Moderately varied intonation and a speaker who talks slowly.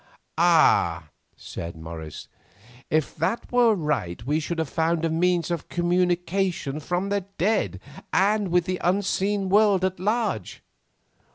Yes: average, 4.4 semitones; slow, 130 wpm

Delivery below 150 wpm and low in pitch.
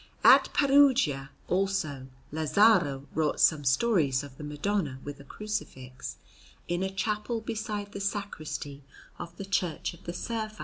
No: average, 140 wpm; medium, 175 Hz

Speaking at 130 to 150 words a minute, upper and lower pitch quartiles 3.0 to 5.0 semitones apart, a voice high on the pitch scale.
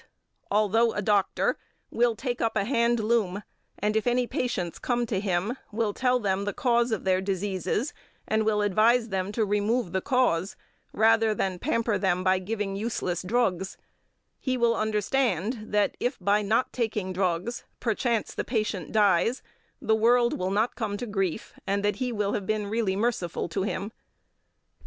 No: average, 170 wpm; average, 3.3 semitones; high, 215 Hz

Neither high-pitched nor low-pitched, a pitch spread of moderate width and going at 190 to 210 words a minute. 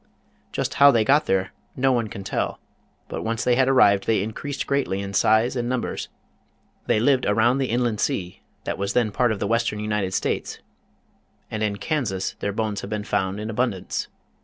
No: low, 110 Hz; average, 3.6 semitones; average, 195 wpm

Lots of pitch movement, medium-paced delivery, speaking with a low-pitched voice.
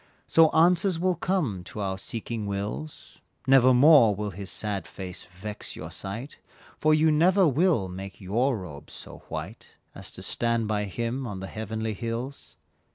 Yes: wide, 7.2 semitones; average, 160 wpm; low, 115 Hz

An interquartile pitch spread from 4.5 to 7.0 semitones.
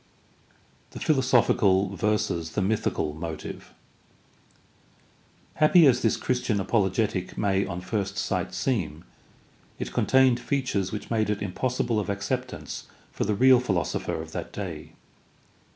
Yes: average, 4.9 semitones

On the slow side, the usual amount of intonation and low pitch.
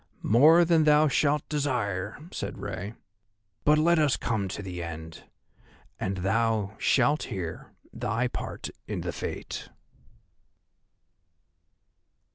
No: slow, 110 wpm; wide, 7.5 semitones; low, 115 Hz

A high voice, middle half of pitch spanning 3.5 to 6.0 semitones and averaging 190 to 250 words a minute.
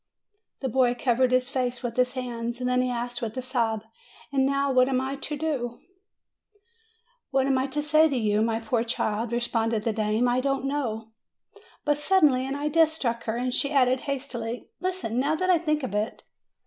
No: very high, 255 Hz; average, 2.9 semitones; average, 200 wpm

